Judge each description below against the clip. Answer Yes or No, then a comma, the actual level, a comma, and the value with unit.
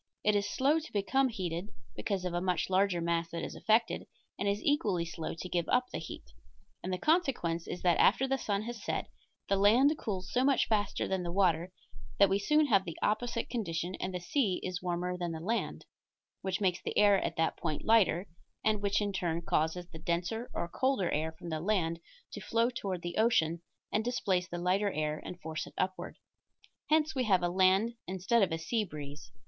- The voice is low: No, high, 190 Hz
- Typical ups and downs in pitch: Yes, average, 4.2 semitones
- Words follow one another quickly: Yes, fast, 210 wpm